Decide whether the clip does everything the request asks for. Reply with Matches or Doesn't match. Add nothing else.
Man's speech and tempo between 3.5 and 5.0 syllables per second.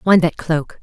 Doesn't match